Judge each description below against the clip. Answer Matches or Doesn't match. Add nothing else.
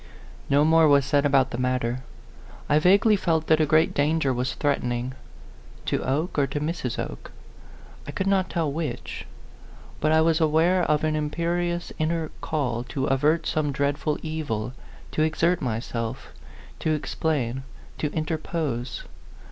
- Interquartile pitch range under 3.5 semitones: Matches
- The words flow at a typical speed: Matches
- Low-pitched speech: Doesn't match